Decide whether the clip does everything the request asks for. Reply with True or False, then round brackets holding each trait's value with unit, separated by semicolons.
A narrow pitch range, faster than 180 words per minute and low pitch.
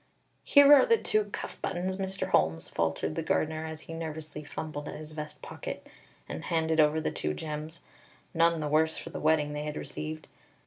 False (1.8 semitones; 190 wpm; 155 Hz)